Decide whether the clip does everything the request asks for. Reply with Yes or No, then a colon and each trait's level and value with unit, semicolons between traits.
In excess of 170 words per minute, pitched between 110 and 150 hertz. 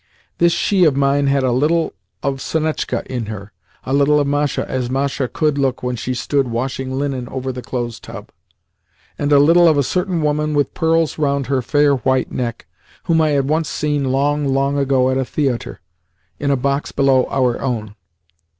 Yes: average, 190 wpm; medium, 140 Hz